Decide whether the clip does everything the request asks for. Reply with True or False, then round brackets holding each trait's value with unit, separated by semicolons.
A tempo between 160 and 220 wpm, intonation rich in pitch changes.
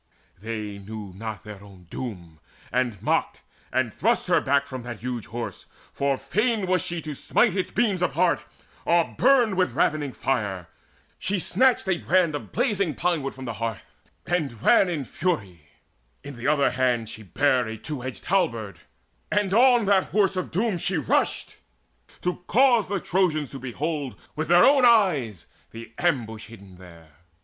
True (165 wpm; 8.5 semitones)